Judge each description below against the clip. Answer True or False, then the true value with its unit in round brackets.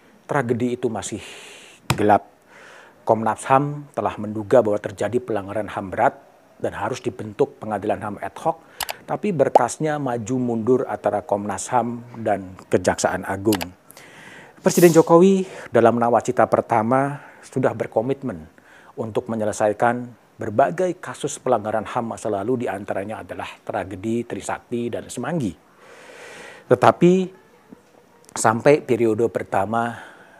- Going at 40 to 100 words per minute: False (110 wpm)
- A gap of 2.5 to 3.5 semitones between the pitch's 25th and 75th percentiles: False (4.1 semitones)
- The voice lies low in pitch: True (115 Hz)